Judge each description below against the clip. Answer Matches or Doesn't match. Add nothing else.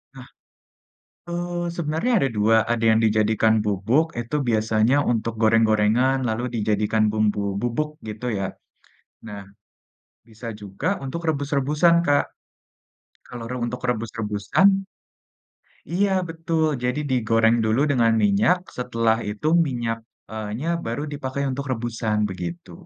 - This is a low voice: Matches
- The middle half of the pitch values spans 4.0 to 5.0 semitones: Matches